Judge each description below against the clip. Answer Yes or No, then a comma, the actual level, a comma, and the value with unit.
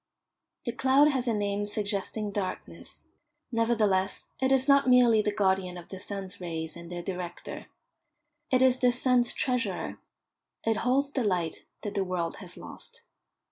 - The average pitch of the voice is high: Yes, high, 210 Hz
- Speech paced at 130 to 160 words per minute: Yes, average, 155 wpm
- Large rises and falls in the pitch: No, average, 5.0 semitones